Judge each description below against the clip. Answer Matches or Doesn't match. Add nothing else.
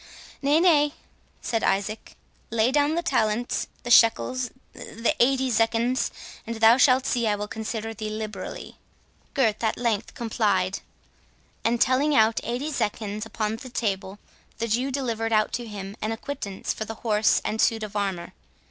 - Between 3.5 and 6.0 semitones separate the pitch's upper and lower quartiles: Doesn't match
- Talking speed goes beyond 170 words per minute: Doesn't match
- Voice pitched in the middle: Doesn't match